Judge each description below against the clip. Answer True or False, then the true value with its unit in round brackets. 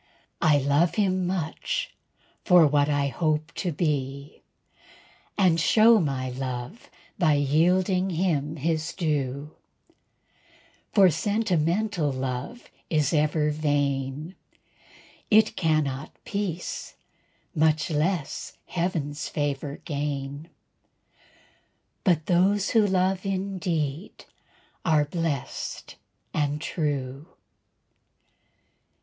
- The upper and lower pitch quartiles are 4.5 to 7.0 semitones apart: False (4.0 semitones)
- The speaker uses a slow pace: True (90 wpm)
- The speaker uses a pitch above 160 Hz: False (155 Hz)